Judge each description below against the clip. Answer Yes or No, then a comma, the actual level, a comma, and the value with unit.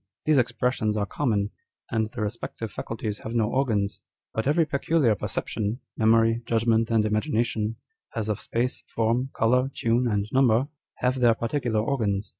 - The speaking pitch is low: Yes, low, 115 Hz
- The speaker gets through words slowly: No, average, 160 wpm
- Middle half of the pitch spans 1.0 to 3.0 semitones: Yes, narrow, 2.6 semitones